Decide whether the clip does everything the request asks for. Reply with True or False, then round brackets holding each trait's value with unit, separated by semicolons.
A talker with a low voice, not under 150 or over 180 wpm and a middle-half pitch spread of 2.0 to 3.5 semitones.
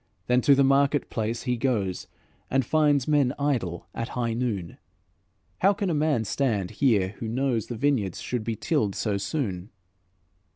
False (125 Hz; 165 wpm; 4.6 semitones)